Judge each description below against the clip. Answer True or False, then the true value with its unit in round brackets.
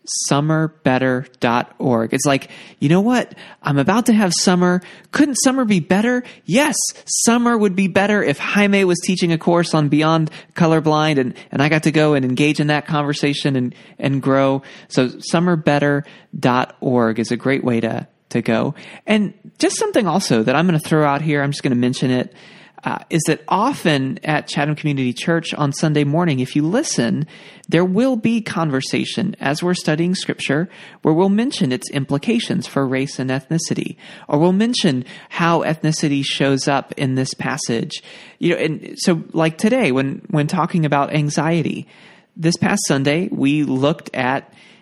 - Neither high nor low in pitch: True (155 Hz)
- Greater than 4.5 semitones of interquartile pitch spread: True (5.5 semitones)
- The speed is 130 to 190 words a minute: True (170 wpm)